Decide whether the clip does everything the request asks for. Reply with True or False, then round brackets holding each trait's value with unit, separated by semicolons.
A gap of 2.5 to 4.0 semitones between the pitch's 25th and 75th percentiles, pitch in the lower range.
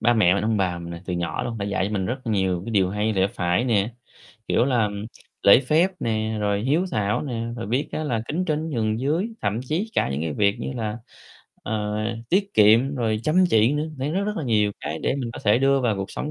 False (5.2 semitones; 110 Hz)